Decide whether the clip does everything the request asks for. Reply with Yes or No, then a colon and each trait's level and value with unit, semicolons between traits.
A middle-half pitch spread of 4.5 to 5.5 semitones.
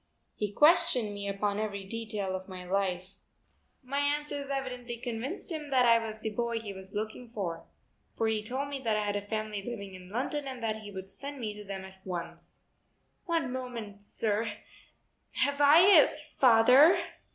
Yes: average, 4.9 semitones